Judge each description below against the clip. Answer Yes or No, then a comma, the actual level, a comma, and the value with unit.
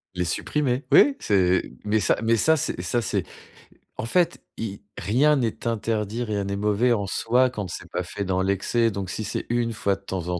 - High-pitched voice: No, low, 105 Hz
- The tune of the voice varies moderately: Yes, average, 3.7 semitones